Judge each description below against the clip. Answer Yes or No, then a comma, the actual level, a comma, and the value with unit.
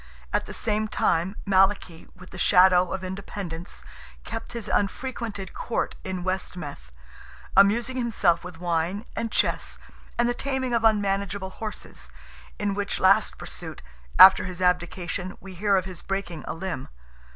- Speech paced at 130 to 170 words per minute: Yes, average, 150 wpm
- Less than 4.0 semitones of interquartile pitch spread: Yes, narrow, 2.6 semitones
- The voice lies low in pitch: No, high, 190 Hz